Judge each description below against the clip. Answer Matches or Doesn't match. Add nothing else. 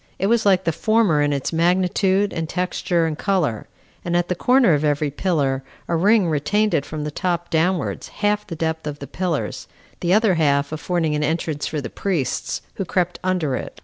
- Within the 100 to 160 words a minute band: Doesn't match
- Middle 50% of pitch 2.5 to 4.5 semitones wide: Matches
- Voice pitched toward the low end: Doesn't match